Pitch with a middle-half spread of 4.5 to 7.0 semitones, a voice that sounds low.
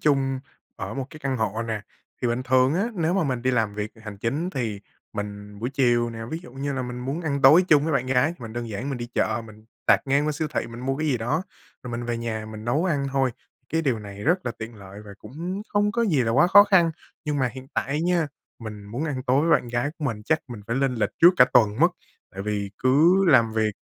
Yes: average, 4.9 semitones; low, 130 Hz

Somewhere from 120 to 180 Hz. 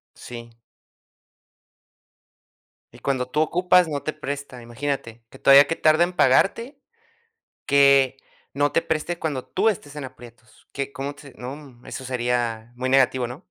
Yes: medium, 140 Hz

